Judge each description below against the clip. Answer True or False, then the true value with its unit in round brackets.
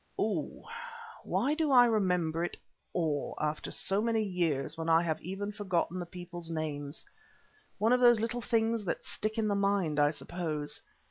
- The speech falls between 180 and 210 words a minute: False (170 wpm)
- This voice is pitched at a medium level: True (180 Hz)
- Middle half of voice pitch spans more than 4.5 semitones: True (5.1 semitones)